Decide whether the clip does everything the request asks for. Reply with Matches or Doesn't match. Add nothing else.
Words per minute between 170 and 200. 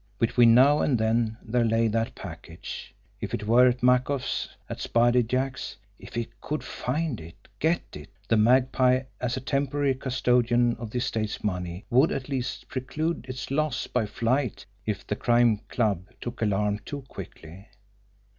Doesn't match